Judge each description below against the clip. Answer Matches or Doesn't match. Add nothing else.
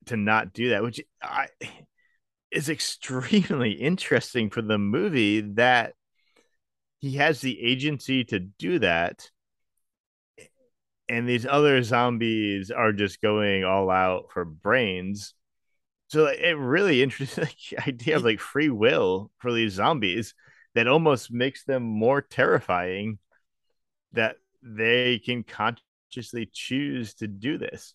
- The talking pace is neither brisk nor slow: Doesn't match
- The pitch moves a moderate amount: Matches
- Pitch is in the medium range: Doesn't match